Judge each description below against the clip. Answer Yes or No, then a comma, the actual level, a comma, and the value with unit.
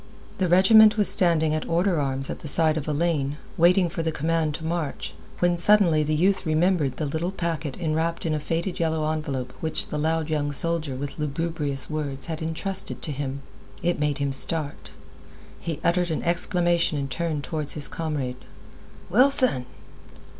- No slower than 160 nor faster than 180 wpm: Yes, average, 175 wpm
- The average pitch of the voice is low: No, medium, 160 Hz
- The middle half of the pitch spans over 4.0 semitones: No, average, 2.7 semitones